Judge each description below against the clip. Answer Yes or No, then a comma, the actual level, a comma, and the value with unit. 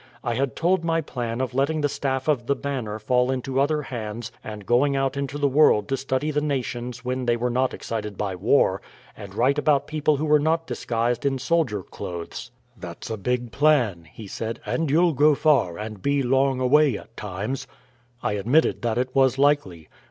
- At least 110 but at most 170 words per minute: No, average, 195 wpm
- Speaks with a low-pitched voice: Yes, low, 130 Hz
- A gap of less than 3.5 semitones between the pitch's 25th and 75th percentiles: No, average, 4.0 semitones